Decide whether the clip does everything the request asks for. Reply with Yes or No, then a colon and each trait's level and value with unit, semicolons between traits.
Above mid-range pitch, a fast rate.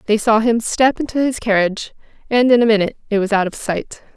Yes: high, 225 Hz; fast, 230 wpm